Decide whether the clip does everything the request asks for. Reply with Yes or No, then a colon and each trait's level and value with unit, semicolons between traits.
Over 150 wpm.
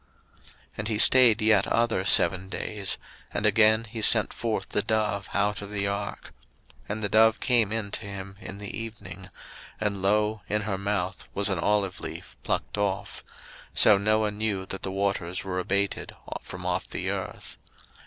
Yes: average, 175 wpm